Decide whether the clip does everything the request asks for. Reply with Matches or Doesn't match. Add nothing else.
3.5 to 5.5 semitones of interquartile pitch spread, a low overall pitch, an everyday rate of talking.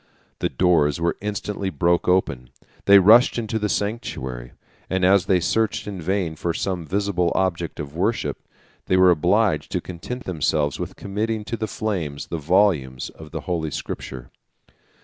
Matches